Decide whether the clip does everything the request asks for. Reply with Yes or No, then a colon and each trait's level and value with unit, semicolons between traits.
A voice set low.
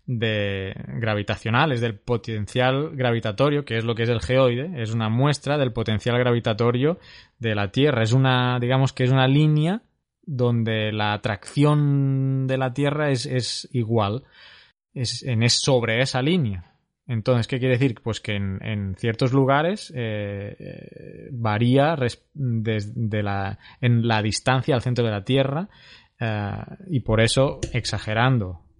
Yes: low, 120 Hz